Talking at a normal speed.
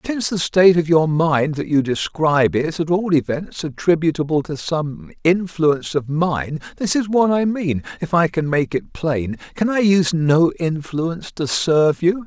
Yes: average, 175 wpm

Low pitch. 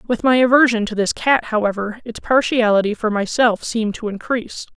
No: high, 225 Hz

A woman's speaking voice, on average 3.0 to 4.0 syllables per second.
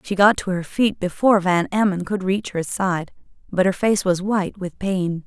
No: female; 4.8 syllables/s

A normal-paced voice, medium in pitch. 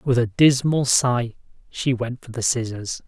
No: average, 175 wpm; low, 125 Hz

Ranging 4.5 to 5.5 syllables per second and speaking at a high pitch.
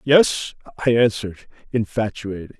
No: 5.1 syllables/s; low, 115 Hz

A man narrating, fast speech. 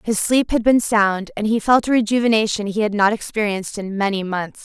No: female; fast, 220 wpm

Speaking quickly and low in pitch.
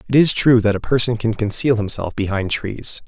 Yes: fast, 215 wpm; low, 110 Hz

